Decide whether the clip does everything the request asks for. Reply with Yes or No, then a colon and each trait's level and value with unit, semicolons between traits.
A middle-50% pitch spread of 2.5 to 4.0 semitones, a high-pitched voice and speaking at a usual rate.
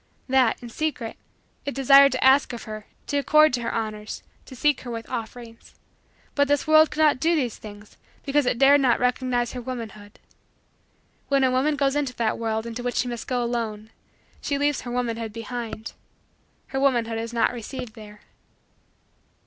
Yes: average, 3.3 semitones; high, 245 Hz; average, 180 wpm